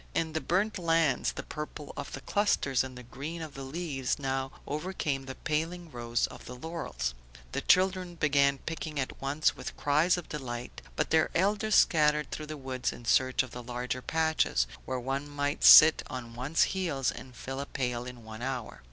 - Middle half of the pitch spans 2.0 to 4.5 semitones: Yes, average, 4.0 semitones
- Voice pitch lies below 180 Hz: Yes, medium, 140 Hz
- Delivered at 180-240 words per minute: Yes, average, 190 wpm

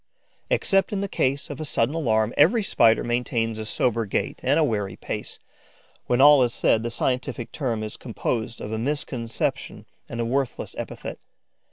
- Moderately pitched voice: No, low, 120 Hz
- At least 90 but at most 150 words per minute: No, average, 175 wpm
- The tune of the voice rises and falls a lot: No, average, 3.8 semitones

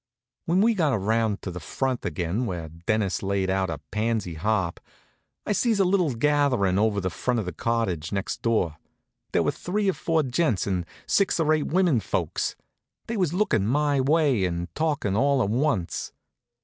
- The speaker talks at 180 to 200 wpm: Yes, average, 185 wpm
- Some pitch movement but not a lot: No, wide, 8.1 semitones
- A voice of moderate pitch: No, low, 115 Hz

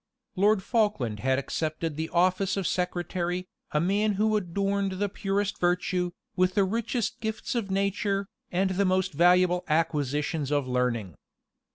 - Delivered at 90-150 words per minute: Yes, average, 145 wpm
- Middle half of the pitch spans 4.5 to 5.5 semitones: No, average, 3.5 semitones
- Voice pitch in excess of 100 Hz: Yes, medium, 185 Hz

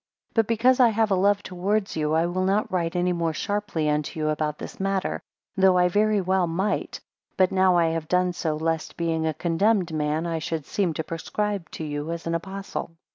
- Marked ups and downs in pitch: No, average, 3.3 semitones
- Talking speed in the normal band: No, fast, 215 wpm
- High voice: No, medium, 175 Hz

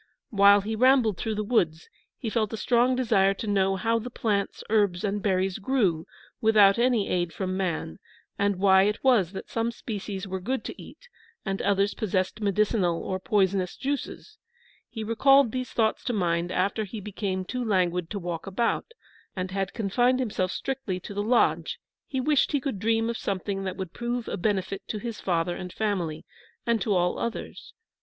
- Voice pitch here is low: No, high, 205 Hz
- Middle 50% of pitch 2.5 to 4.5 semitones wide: Yes, average, 3.5 semitones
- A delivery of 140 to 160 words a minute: No, average, 185 wpm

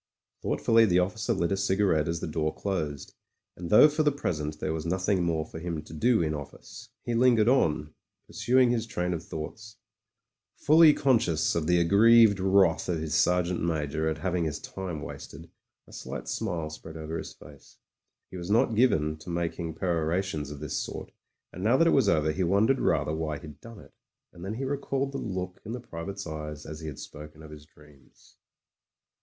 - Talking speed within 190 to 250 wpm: Yes, average, 195 wpm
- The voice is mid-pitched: No, very low, 85 Hz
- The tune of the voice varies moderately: No, wide, 5.8 semitones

